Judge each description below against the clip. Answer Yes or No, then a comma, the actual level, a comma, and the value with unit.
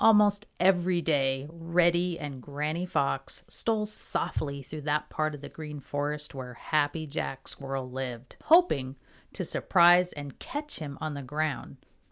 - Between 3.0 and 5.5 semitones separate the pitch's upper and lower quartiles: Yes, average, 3.9 semitones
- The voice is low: No, medium, 150 Hz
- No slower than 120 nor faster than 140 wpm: No, average, 150 wpm